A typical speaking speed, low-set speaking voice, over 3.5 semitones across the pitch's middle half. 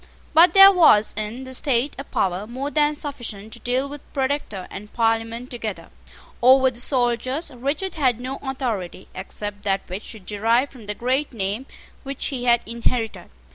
No: average, 170 wpm; high, 245 Hz; average, 4.1 semitones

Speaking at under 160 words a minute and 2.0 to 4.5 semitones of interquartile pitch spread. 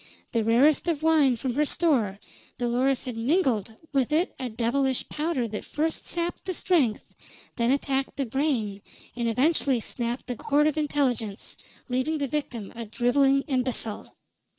Yes: average, 150 wpm; average, 4.1 semitones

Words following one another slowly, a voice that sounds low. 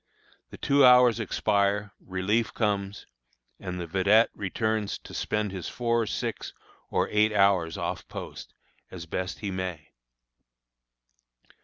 Yes: slow, 125 wpm; low, 100 Hz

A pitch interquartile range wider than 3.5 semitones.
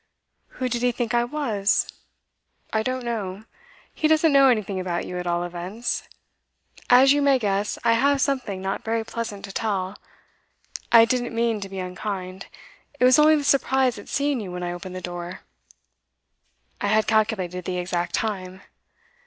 Yes: average, 5.2 semitones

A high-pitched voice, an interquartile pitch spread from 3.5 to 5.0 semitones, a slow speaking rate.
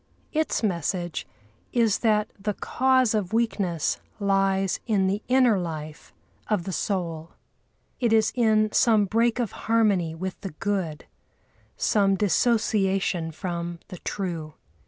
Yes: high, 195 Hz; average, 4.0 semitones; slow, 125 wpm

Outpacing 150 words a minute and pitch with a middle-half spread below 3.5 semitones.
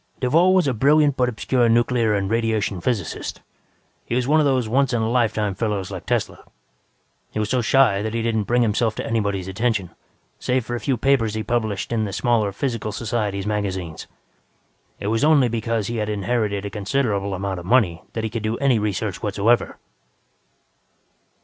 Yes: average, 185 wpm; average, 3.1 semitones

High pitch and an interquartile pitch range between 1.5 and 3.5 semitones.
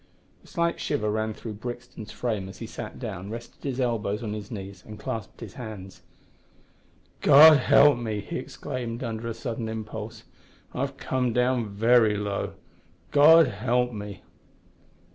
No: low, 115 Hz; average, 3.1 semitones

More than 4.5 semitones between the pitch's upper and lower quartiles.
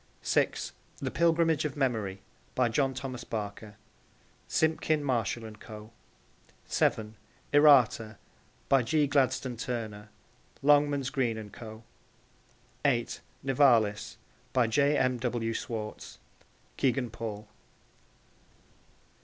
No: average, 4.1 semitones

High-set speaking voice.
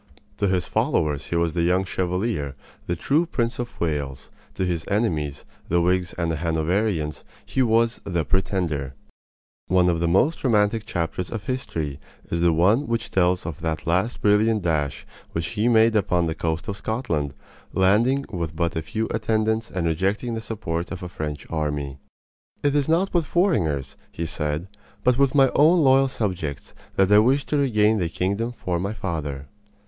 No: very low, 95 Hz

